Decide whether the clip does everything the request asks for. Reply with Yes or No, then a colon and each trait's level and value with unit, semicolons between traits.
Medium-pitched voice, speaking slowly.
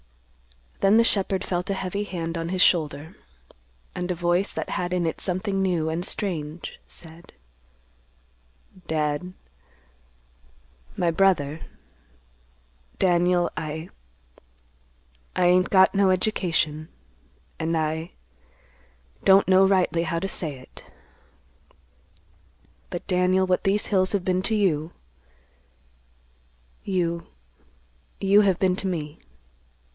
Yes: medium, 165 Hz; slow, 100 wpm